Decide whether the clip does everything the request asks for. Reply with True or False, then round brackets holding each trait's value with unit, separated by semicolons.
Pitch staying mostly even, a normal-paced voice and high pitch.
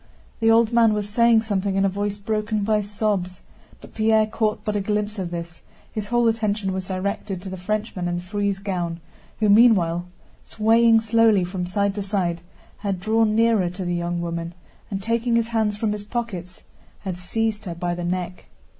False (3.3 semitones; 190 wpm; 205 Hz)